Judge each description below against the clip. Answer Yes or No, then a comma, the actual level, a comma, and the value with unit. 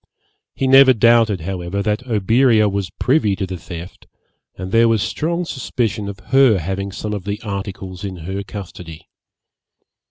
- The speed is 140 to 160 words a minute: Yes, average, 155 wpm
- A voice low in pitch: Yes, low, 100 Hz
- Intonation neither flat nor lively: Yes, average, 3.6 semitones